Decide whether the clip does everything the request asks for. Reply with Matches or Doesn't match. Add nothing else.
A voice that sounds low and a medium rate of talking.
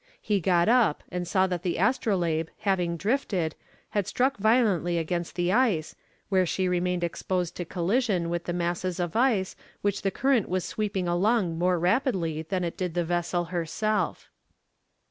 Doesn't match